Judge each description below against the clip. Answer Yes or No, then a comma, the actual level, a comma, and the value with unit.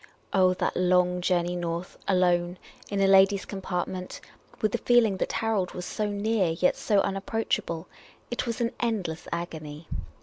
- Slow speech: No, average, 165 wpm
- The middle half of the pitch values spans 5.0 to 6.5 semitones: No, narrow, 2.6 semitones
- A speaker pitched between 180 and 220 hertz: Yes, medium, 185 Hz